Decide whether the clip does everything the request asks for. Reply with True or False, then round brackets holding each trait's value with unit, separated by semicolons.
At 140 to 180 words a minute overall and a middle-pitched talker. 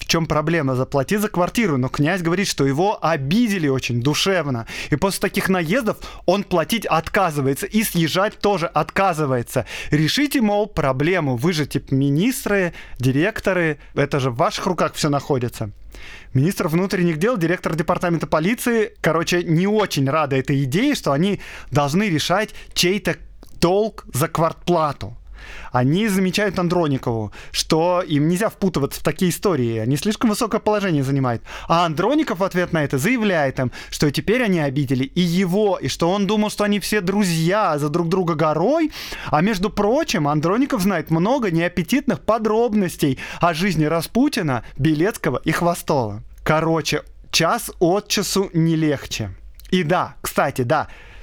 True (145 wpm; 170 Hz)